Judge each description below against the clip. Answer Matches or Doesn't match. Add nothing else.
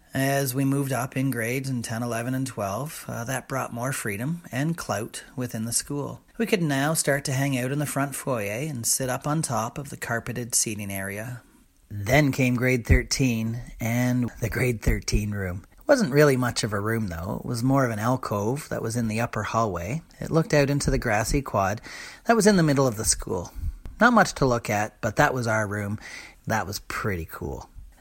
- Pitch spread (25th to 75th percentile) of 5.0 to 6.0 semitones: Doesn't match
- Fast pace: Matches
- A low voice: Matches